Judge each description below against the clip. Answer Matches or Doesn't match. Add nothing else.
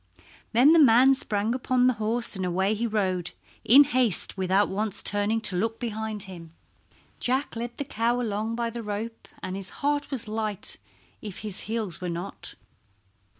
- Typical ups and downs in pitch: Matches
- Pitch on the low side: Doesn't match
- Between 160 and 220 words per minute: Matches